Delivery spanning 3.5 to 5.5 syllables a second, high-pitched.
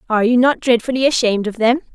No: 7.2 syllables/s; high, 240 Hz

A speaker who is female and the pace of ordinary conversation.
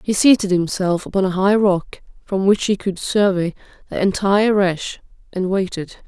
Yes: female; average, 170 wpm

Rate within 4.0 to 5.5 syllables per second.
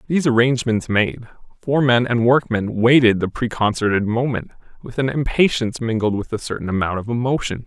No: 5.9 syllables/s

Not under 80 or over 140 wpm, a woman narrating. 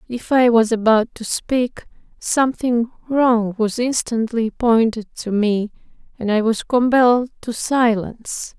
Yes: slow, 135 wpm; female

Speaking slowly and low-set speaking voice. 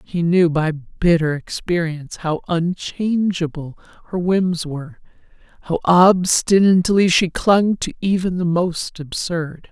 No: slow, 115 wpm; medium, 175 Hz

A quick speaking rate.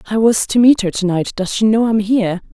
Yes: fast, 280 wpm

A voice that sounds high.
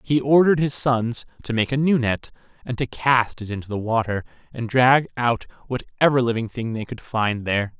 No: low, 120 Hz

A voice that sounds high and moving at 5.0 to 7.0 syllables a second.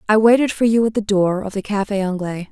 Yes: high, 205 Hz; 6.0 syllables/s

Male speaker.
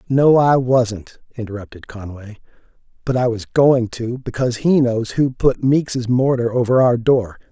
Yes: male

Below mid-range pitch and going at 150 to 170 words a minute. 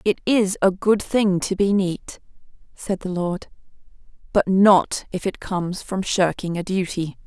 No: high, 190 Hz; average, 165 wpm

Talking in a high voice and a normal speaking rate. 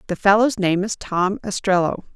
Yes: high, 195 Hz; average, 165 wpm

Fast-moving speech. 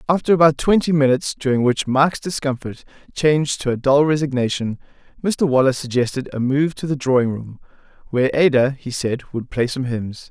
No: average, 175 wpm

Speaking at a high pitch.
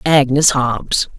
No: low, 135 Hz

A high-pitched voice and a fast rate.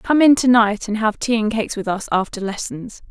Yes: high, 220 Hz; fast, 250 wpm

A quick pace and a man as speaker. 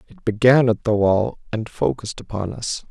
No: average, 185 wpm; male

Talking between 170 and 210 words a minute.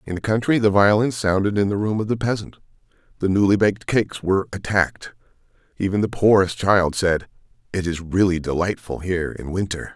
Yes: average, 180 wpm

